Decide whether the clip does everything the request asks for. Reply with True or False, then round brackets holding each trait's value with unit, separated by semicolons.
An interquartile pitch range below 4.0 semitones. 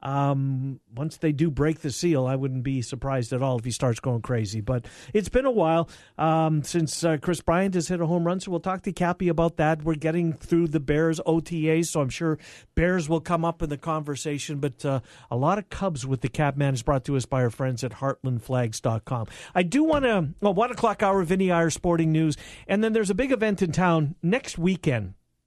False (4.5 semitones)